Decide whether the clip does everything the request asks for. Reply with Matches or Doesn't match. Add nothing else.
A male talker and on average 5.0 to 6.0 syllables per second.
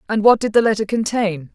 Doesn't match